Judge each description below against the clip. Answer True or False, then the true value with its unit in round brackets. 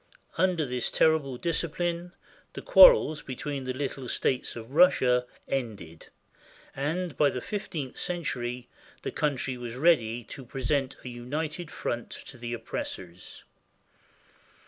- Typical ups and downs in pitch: True (4.6 semitones)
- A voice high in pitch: False (135 Hz)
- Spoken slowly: True (130 wpm)